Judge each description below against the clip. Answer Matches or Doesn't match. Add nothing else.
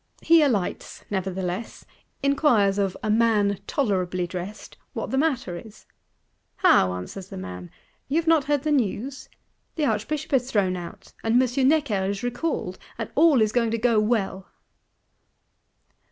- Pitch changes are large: Matches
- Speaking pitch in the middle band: Doesn't match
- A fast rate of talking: Doesn't match